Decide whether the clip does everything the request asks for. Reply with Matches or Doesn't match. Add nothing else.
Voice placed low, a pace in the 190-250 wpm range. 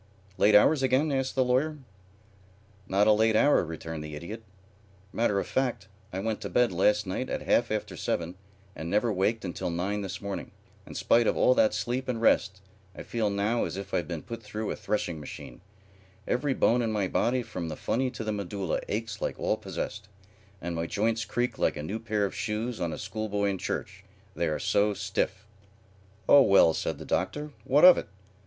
Matches